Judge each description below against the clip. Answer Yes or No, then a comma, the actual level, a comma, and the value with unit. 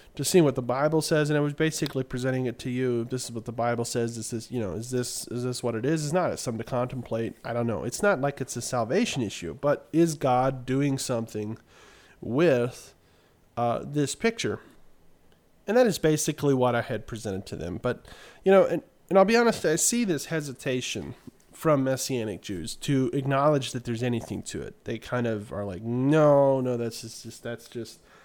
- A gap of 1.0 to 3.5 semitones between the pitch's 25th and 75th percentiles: No, average, 4.0 semitones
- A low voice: Yes, low, 125 Hz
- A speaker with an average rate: No, fast, 210 wpm